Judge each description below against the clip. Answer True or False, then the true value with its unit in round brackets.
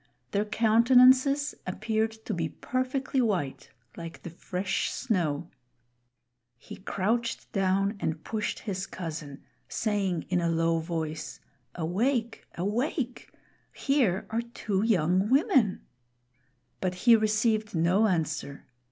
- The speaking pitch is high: True (200 Hz)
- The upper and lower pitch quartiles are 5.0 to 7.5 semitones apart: True (5.3 semitones)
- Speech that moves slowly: True (110 wpm)